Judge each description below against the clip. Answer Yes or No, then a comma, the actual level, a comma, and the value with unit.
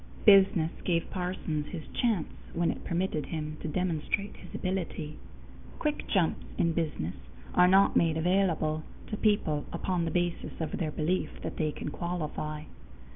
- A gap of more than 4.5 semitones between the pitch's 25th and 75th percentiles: No, average, 3.2 semitones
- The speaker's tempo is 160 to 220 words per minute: No, average, 150 wpm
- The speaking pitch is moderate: Yes, medium, 170 Hz